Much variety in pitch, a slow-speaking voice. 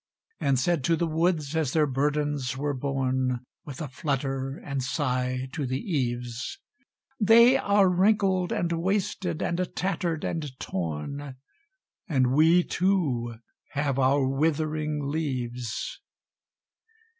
No: average, 4.4 semitones; slow, 120 wpm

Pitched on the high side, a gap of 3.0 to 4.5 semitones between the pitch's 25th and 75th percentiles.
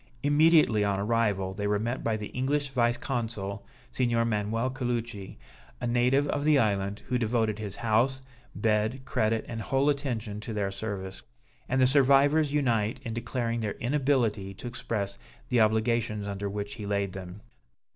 No: low, 115 Hz; average, 3.7 semitones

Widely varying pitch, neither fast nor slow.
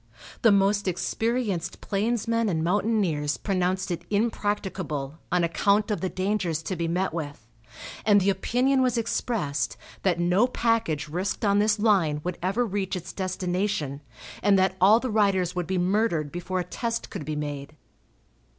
No: average, 3.7 semitones; average, 160 wpm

